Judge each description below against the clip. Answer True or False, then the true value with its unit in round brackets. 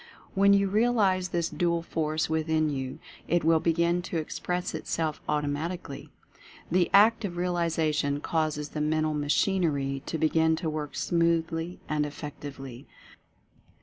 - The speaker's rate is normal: False (130 wpm)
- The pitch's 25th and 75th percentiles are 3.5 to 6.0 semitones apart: False (2.7 semitones)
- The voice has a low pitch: False (160 Hz)